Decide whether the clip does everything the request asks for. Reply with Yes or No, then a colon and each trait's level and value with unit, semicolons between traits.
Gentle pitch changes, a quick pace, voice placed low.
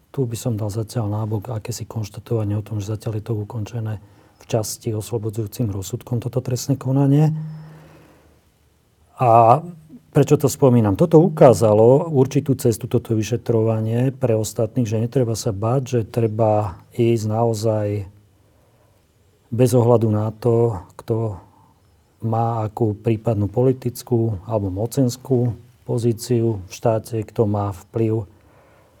No: narrow, 2.3 semitones; average, 120 wpm; low, 115 Hz